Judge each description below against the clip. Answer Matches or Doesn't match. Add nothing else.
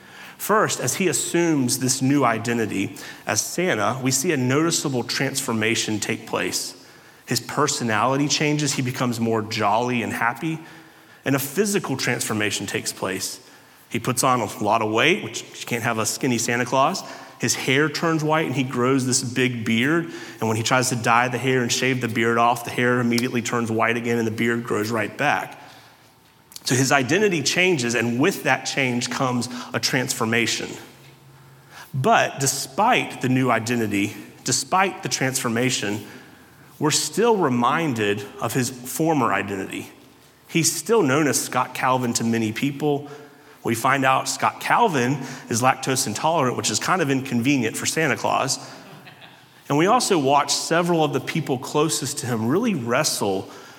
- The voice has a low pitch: Matches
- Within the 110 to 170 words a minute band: Matches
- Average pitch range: Matches